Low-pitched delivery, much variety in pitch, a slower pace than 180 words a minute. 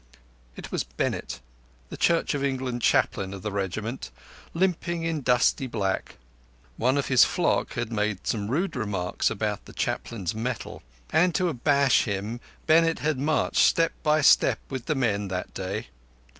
Yes: low, 125 Hz; wide, 6.5 semitones; average, 155 wpm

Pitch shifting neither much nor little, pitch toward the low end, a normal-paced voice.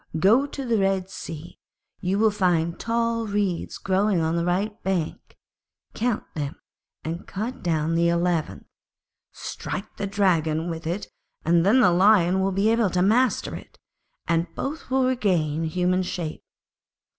No: average, 4.0 semitones; medium, 185 Hz; average, 150 wpm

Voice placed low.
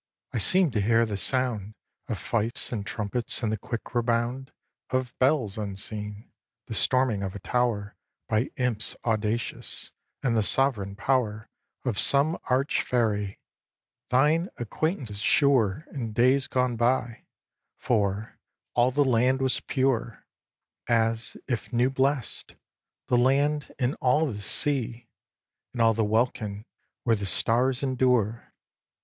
Yes: low, 120 Hz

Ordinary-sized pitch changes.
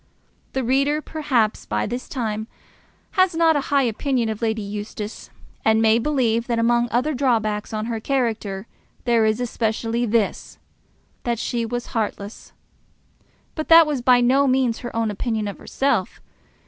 Yes: average, 3.3 semitones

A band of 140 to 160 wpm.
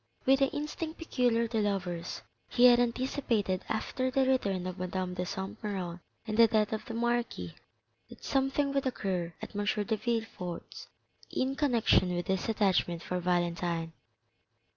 Yes: average, 155 wpm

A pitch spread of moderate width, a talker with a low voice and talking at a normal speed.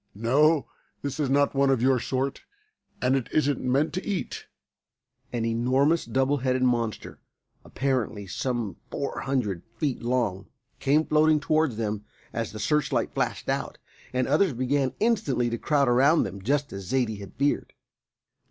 Yes: average, 3.6 semitones; low, 130 Hz; average, 150 wpm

